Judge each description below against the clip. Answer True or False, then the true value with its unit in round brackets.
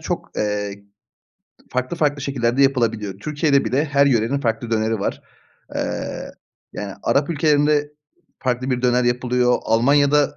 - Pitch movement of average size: True (3.9 semitones)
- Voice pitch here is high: False (125 Hz)